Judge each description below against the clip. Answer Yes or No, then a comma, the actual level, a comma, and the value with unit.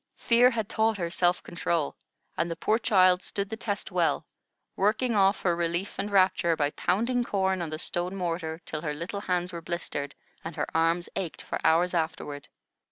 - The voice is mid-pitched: Yes, medium, 180 Hz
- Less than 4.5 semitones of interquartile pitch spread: Yes, average, 3.2 semitones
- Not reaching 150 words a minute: No, average, 185 wpm